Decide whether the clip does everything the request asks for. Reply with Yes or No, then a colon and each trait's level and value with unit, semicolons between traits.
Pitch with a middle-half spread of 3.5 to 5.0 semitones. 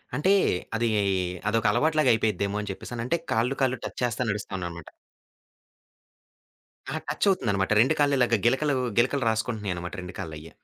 Yes: average, 4.4 semitones